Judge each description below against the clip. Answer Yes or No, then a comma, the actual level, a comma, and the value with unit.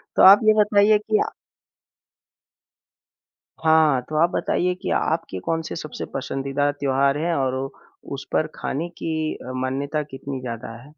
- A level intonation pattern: No, average, 3.6 semitones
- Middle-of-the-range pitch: Yes, medium, 150 Hz